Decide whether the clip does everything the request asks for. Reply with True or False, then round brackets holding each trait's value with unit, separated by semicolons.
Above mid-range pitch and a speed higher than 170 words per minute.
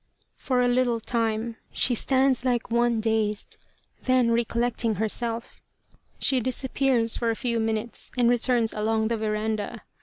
False (235 Hz; 140 wpm)